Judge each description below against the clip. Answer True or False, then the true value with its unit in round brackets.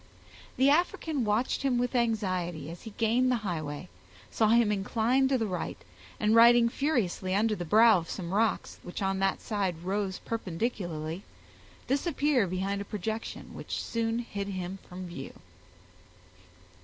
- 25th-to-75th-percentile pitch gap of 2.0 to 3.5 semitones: False (4.3 semitones)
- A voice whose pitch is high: True (210 Hz)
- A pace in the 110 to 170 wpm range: True (150 wpm)